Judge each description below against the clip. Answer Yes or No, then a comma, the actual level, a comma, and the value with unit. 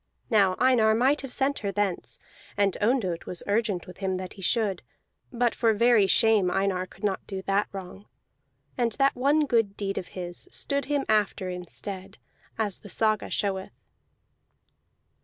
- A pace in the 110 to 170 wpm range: Yes, average, 165 wpm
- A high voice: Yes, high, 205 Hz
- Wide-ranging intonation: No, average, 3.5 semitones